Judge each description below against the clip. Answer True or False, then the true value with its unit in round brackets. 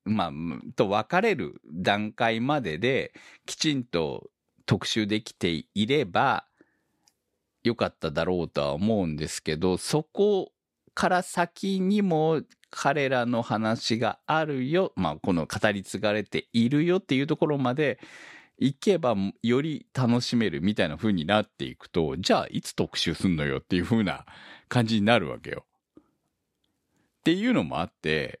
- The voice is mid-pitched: False (120 Hz)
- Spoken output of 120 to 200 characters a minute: False (285 characters per minute)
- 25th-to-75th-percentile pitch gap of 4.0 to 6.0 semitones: False (7.0 semitones)